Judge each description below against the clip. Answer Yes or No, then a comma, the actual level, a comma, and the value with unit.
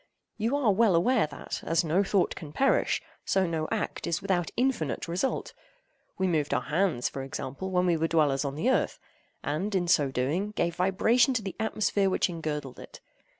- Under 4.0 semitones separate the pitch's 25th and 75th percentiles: No, average, 4.7 semitones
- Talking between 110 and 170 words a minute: No, average, 190 wpm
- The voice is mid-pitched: Yes, medium, 175 Hz